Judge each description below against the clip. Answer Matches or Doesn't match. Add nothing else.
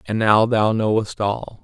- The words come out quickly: Doesn't match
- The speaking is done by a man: Matches